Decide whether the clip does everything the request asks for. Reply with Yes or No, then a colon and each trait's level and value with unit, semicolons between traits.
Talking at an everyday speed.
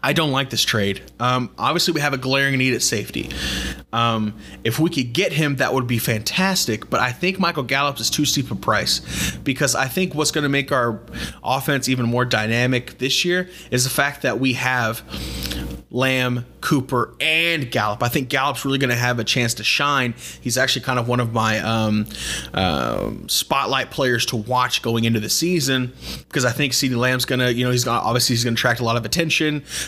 No: fast, 215 wpm